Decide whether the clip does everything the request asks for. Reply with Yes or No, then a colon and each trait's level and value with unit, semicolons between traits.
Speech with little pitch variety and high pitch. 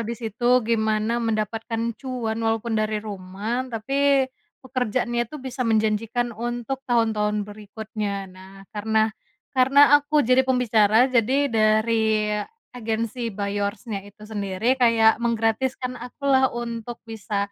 Yes: narrow, 2.2 semitones; high, 225 Hz